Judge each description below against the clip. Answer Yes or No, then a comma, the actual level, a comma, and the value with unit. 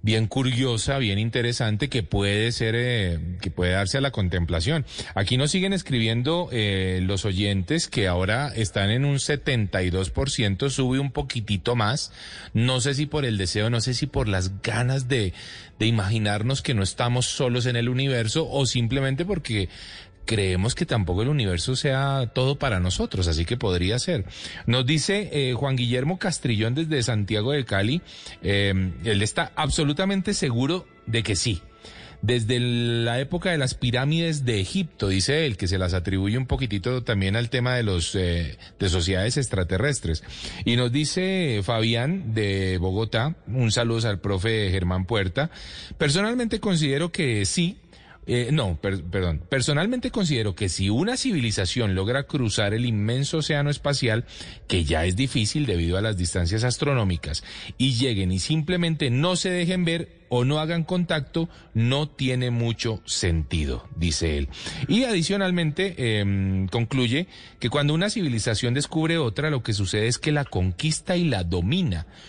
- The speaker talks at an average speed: Yes, average, 160 wpm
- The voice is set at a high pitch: No, low, 120 Hz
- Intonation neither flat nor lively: No, wide, 6.4 semitones